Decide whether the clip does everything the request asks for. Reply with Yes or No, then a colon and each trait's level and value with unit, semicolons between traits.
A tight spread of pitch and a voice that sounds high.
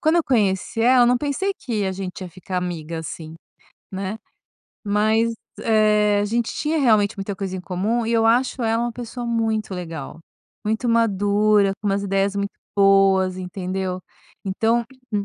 No: average, 3.2 semitones; high, 205 Hz